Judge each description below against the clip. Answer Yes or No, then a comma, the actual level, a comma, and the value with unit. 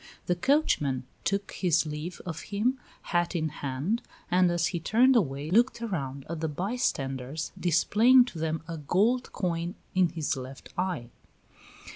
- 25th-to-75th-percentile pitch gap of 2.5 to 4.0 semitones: No, average, 5.2 semitones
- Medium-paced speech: Yes, average, 150 wpm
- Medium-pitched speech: Yes, medium, 175 Hz